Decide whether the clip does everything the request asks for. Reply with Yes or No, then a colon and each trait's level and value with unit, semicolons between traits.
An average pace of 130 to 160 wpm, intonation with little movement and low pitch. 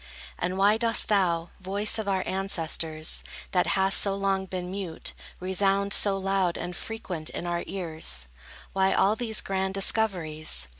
No: average, 150 wpm; narrow, 2.2 semitones; high, 190 Hz